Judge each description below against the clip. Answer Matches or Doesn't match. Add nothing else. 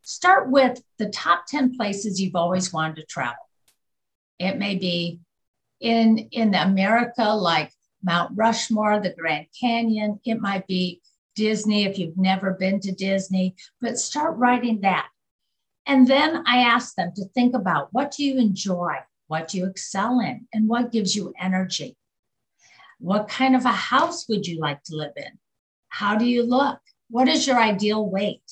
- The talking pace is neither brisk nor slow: Matches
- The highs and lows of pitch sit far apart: Doesn't match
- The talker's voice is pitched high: Matches